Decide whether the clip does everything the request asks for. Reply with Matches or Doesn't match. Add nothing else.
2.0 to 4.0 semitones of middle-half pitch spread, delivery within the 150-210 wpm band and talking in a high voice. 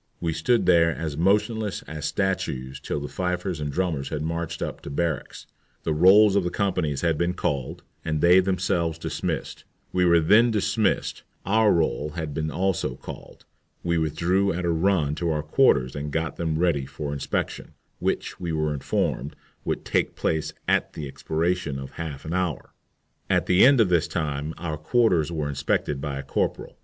Doesn't match